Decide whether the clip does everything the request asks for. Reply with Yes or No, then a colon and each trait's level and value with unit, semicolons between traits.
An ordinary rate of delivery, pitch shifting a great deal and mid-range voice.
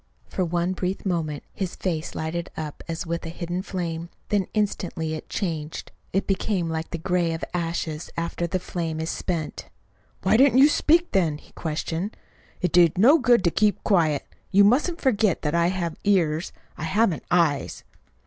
No: average, 175 wpm; average, 3.2 semitones; medium, 175 Hz